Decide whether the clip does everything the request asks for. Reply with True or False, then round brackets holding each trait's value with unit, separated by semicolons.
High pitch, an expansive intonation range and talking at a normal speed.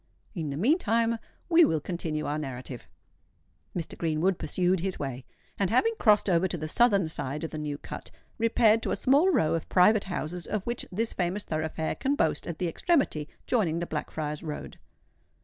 False (175 Hz; 6.2 semitones; 185 wpm)